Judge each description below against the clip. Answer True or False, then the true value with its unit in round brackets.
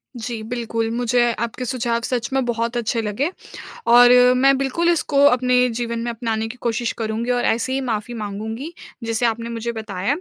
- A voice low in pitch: False (235 Hz)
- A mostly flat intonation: True (1.8 semitones)